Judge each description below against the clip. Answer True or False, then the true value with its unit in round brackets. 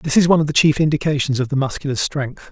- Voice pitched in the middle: True (145 Hz)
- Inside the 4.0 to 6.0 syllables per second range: False (6.9 syllables/s)